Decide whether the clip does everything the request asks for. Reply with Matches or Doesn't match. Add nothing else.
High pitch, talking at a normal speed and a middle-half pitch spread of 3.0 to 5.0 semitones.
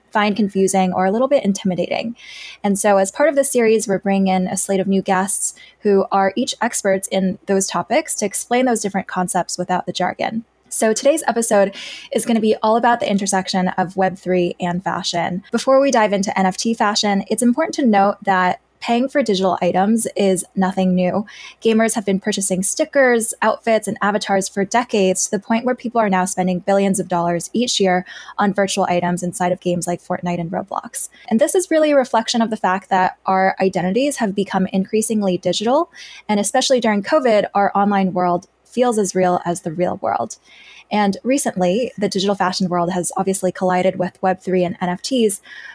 Matches